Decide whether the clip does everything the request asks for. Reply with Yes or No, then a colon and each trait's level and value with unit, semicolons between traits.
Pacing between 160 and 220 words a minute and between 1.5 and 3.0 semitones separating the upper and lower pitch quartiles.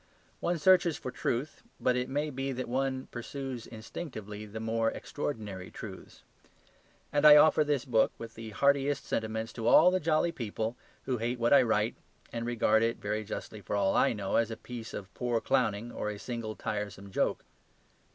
No: average, 180 wpm; average, 3.7 semitones